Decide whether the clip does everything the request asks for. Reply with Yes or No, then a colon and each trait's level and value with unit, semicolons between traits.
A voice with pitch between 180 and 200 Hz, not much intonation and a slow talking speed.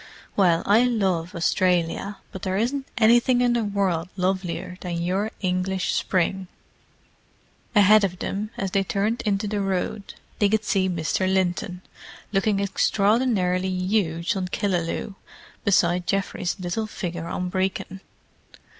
Yes: high, 190 Hz; narrow, 2.3 semitones; slow, 130 wpm